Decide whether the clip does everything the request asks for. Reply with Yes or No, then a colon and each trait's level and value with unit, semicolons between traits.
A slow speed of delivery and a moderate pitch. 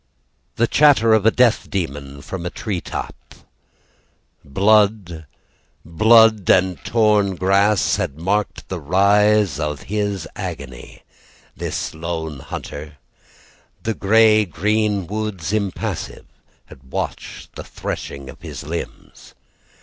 No: slow, 110 wpm; very low, 95 Hz